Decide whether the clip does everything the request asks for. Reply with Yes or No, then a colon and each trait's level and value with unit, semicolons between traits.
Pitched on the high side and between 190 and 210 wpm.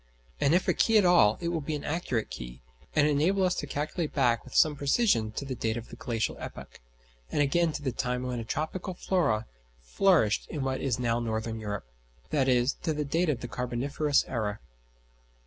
No: low, 135 Hz; average, 200 wpm